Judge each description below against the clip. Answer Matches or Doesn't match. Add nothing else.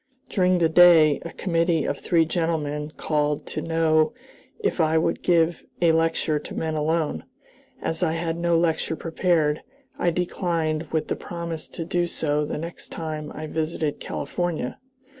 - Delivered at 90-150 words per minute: Doesn't match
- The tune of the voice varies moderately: Doesn't match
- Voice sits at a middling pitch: Matches